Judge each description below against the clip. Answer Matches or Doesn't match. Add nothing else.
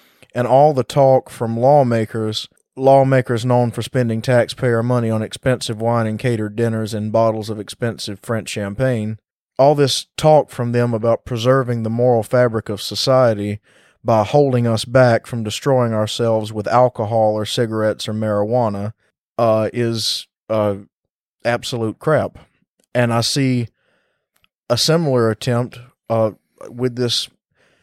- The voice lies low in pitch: Matches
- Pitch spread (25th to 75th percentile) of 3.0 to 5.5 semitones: Doesn't match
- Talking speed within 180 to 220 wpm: Doesn't match